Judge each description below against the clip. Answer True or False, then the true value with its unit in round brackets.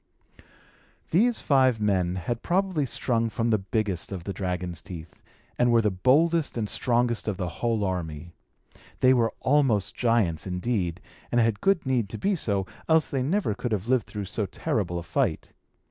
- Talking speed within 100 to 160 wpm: False (175 wpm)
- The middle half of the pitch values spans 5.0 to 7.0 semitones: True (5.5 semitones)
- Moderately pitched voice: False (110 Hz)